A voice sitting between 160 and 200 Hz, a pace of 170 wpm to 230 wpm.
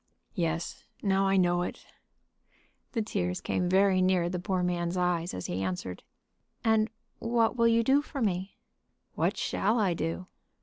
No: medium, 185 Hz; average, 160 wpm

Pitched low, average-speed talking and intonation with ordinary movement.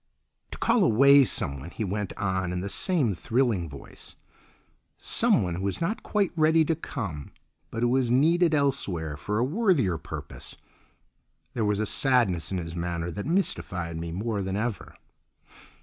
No: low, 105 Hz; average, 160 wpm; wide, 7.9 semitones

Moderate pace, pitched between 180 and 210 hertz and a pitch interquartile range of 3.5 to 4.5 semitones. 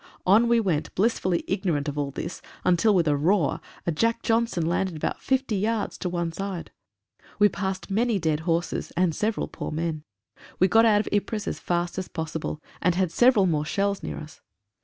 Yes: average, 190 wpm; medium, 185 Hz; average, 4.1 semitones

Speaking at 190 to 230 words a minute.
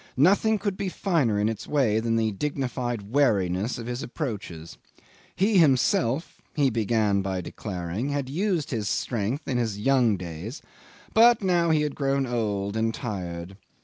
No: average, 155 wpm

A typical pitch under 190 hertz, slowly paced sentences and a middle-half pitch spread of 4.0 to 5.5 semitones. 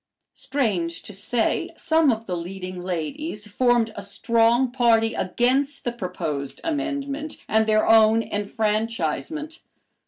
No: high, 225 Hz; slow, 120 wpm; average, 5.2 semitones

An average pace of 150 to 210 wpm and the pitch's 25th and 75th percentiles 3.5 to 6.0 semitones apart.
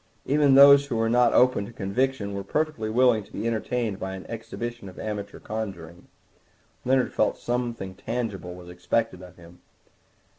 Yes: average, 170 wpm; average, 4.3 semitones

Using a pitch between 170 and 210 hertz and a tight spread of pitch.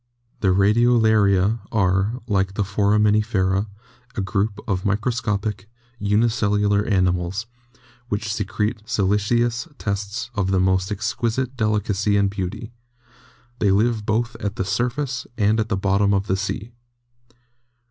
No: low, 105 Hz; narrow, 2.2 semitones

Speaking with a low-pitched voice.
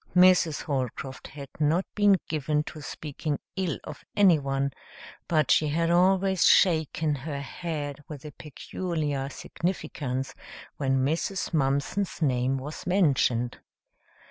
No: medium, 150 Hz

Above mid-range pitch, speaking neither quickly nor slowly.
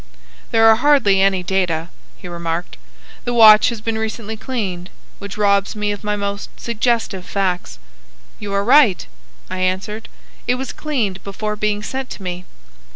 Yes: high, 205 Hz; average, 155 wpm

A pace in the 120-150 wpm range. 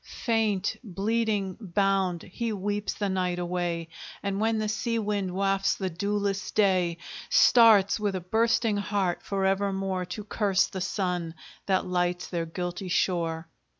Yes: average, 145 wpm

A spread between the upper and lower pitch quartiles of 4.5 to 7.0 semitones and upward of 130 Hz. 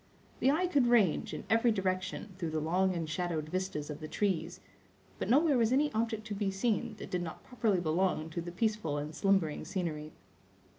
Yes: wide, 5.5 semitones; high, 190 Hz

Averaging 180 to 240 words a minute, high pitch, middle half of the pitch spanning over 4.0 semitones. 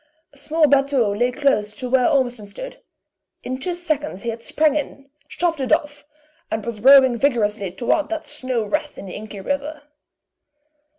No: average, 170 wpm; very high, 265 Hz; average, 4.6 semitones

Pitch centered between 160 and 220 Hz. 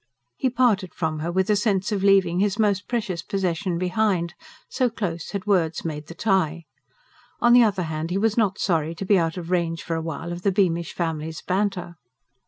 Yes: medium, 185 Hz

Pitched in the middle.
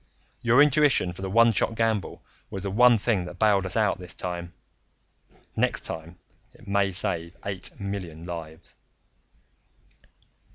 No: low, 100 Hz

